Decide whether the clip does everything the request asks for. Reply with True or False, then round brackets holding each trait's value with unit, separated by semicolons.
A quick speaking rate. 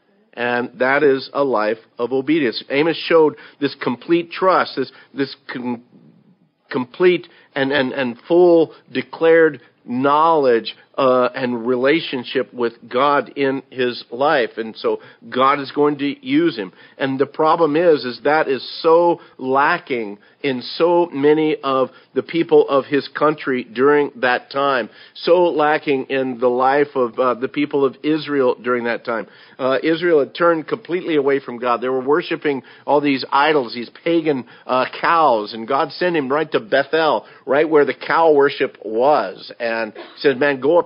False (160 wpm)